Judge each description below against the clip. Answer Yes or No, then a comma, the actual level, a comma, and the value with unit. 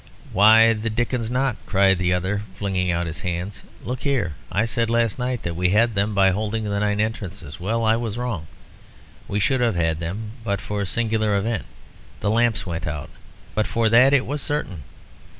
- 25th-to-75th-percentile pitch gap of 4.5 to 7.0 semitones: No, average, 3.7 semitones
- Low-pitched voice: Yes, low, 105 Hz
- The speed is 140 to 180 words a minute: No, average, 195 wpm